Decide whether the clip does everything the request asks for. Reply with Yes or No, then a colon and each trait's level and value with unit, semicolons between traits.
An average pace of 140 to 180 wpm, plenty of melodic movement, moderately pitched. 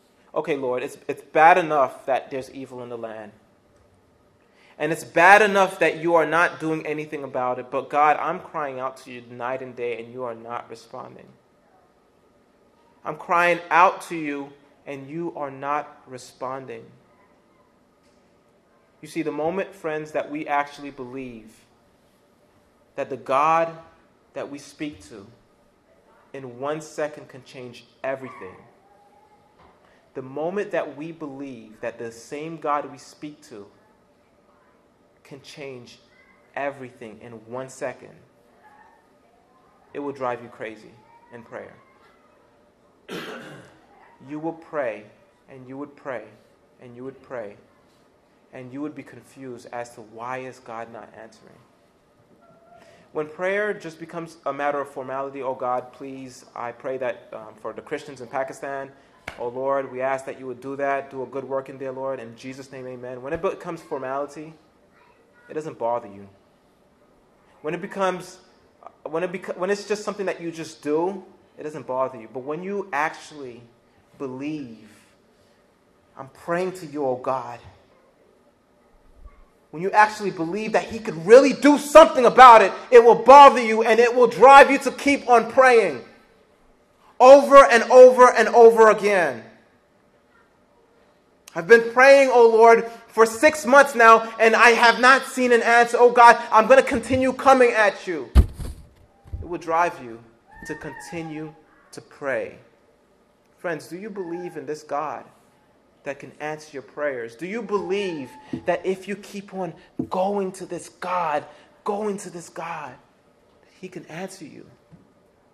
Yes: average, 150 wpm; wide, 7.2 semitones; medium, 150 Hz